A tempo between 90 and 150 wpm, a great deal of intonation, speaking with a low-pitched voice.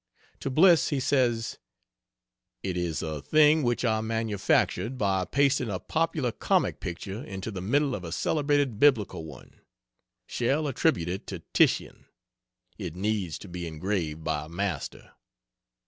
Yes: average, 145 wpm; wide, 7.3 semitones; low, 110 Hz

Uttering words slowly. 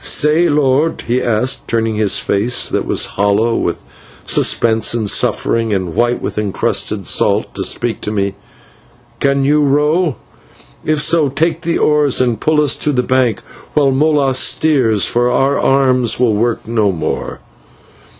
No: average, 155 wpm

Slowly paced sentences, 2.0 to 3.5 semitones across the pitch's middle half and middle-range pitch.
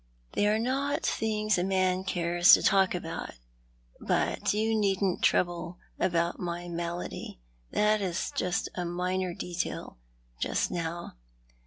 Yes: slow, 130 wpm; average, 2.9 semitones; medium, 180 Hz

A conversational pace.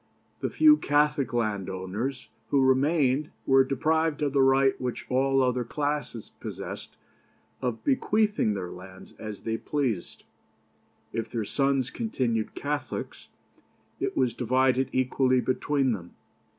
No: slow, 125 wpm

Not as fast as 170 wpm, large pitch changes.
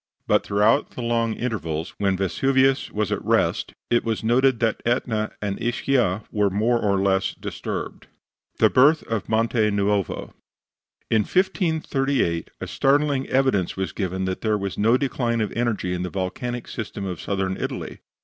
No: average, 160 wpm; average, 4.2 semitones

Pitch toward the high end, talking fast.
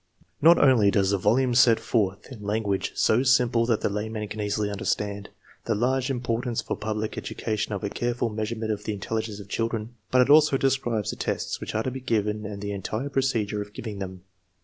No: low, 110 Hz; fast, 215 wpm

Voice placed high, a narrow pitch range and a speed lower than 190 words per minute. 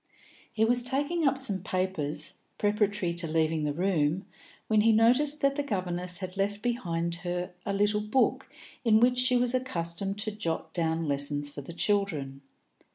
No: high, 195 Hz; wide, 5.4 semitones; average, 165 wpm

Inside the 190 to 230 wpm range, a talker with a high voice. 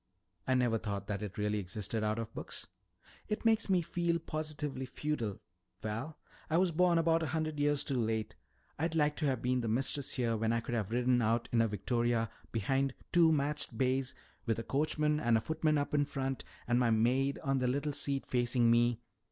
No: average, 200 wpm; low, 130 Hz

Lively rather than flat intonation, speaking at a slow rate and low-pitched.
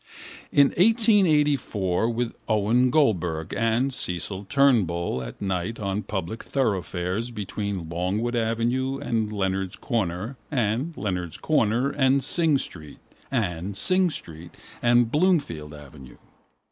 Yes: wide, 6.6 semitones; slow, 110 wpm; low, 110 Hz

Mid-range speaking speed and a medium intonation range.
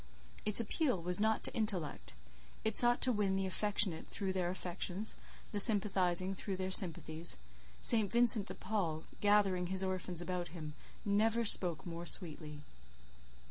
Yes: average, 145 wpm; average, 3.2 semitones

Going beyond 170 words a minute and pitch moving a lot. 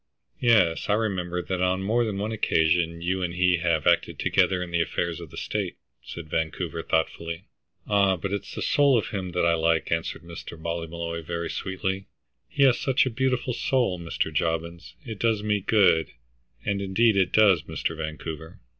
No: average, 180 wpm; average, 3.8 semitones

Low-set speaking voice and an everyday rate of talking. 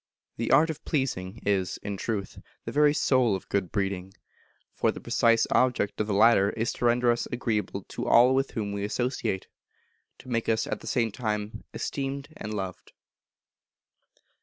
Yes: low, 115 Hz; average, 170 wpm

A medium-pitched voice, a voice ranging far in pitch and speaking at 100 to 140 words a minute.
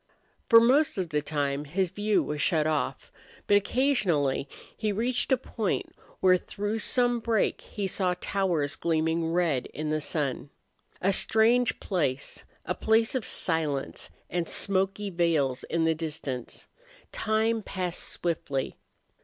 Yes: medium, 180 Hz; wide, 5.9 semitones; slow, 135 wpm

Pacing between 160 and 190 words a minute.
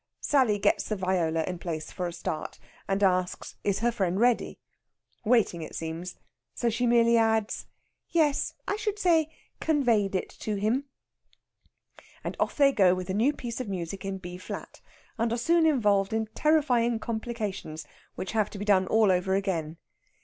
Yes: average, 170 wpm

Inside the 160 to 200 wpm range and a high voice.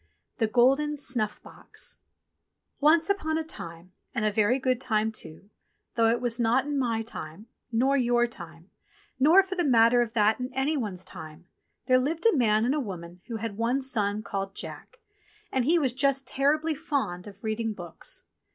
Yes: average, 180 wpm; high, 240 Hz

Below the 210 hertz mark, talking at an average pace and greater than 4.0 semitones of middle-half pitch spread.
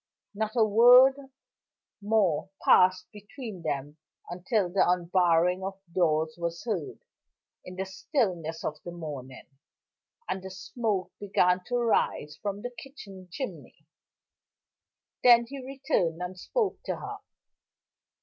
No: high, 190 Hz; slow, 120 wpm; average, 4.6 semitones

